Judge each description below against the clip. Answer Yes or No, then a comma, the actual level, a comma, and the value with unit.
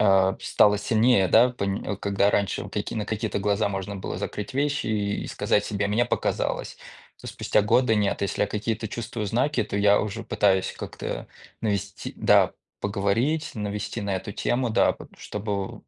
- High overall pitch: No, low, 105 Hz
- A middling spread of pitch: No, narrow, 2.0 semitones